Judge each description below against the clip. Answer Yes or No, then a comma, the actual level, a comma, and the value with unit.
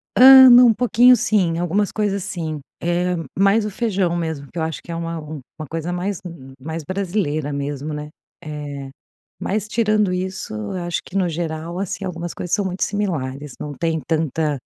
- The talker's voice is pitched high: No, medium, 175 Hz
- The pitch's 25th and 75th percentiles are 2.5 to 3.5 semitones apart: No, average, 4.2 semitones